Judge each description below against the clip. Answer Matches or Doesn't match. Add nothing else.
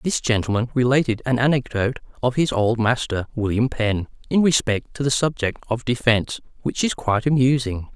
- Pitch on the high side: Doesn't match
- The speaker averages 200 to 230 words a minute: Doesn't match